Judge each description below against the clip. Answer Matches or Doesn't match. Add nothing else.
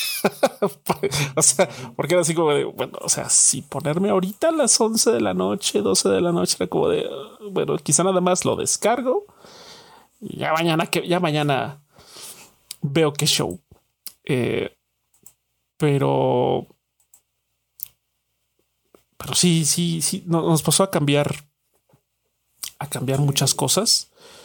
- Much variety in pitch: Matches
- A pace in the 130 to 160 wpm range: Matches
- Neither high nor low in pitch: Matches